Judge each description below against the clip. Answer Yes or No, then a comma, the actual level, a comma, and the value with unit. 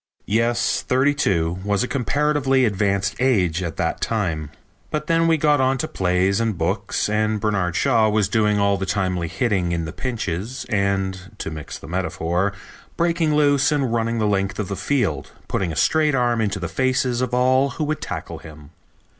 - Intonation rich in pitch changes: Yes, wide, 5.7 semitones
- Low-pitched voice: Yes, low, 105 Hz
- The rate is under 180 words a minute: No, average, 185 wpm